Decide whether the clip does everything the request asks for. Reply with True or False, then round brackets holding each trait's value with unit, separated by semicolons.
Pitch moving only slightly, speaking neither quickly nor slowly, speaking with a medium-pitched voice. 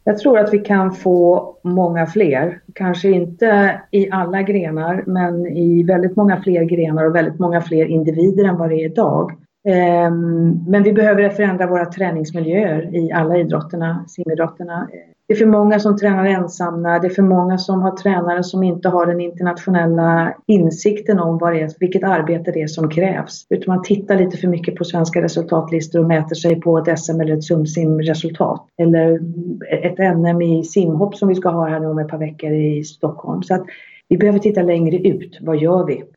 True (2.3 semitones; 185 wpm; 175 Hz)